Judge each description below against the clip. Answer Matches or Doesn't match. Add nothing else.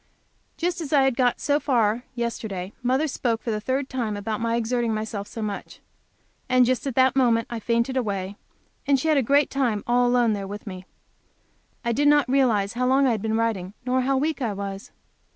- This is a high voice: Matches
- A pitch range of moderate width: Matches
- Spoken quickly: Matches